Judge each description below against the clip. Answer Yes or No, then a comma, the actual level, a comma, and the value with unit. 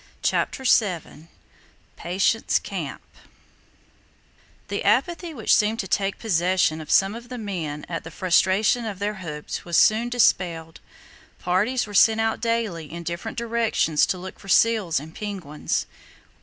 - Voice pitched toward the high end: Yes, high, 195 Hz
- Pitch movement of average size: Yes, average, 4.8 semitones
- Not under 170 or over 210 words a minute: No, average, 140 wpm